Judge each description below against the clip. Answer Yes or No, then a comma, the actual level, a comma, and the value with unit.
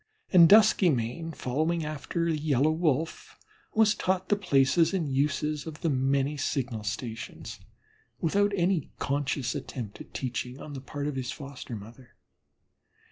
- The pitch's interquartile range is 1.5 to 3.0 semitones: No, average, 4.0 semitones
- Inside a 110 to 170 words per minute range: Yes, average, 140 wpm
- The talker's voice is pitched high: No, medium, 145 Hz